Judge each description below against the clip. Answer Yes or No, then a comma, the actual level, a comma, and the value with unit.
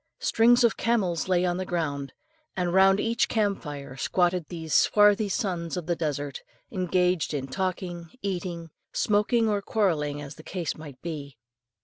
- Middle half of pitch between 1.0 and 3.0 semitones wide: No, average, 4.0 semitones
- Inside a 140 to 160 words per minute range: Yes, average, 155 wpm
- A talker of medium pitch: Yes, medium, 175 Hz